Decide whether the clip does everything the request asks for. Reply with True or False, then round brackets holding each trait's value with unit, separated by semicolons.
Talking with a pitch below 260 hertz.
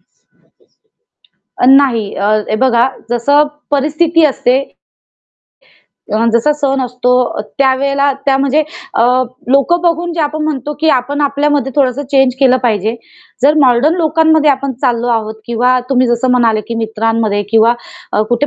False (265 Hz)